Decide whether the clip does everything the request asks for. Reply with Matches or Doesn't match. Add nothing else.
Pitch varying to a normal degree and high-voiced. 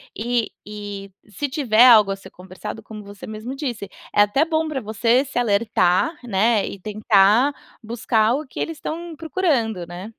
Matches